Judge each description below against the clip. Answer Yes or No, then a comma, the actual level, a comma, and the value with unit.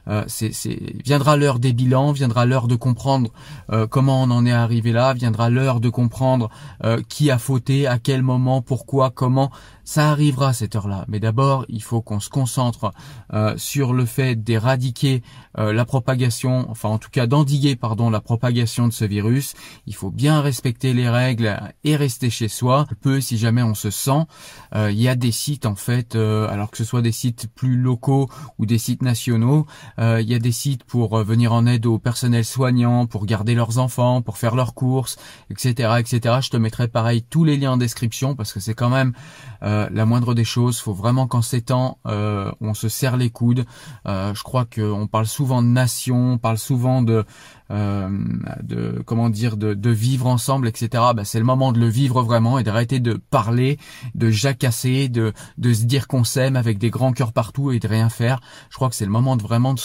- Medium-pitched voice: No, low, 120 Hz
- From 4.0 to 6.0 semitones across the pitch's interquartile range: No, narrow, 2.5 semitones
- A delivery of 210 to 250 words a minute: Yes, average, 215 wpm